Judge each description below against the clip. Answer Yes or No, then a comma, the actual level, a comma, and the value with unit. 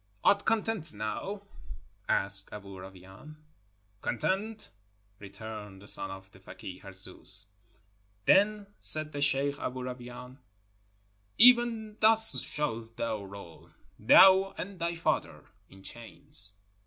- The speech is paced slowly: Yes, slow, 110 wpm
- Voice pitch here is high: No, low, 125 Hz